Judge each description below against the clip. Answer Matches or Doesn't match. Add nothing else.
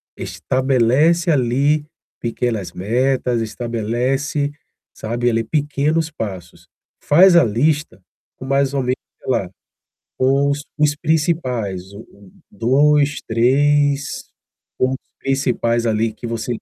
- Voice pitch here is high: Doesn't match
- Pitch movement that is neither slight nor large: Matches